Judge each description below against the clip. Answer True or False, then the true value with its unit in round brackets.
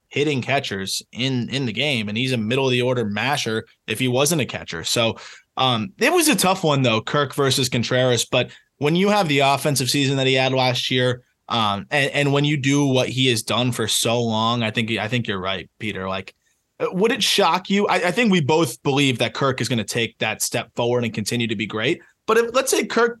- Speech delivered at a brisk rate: True (240 wpm)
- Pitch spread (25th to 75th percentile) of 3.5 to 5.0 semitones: True (3.9 semitones)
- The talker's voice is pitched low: True (125 Hz)